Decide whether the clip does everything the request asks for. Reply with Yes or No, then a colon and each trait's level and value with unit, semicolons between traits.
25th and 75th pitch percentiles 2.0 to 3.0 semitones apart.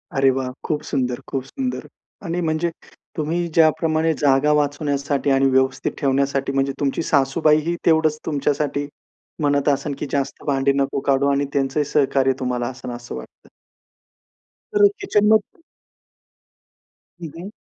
Yes: narrow, 2.6 semitones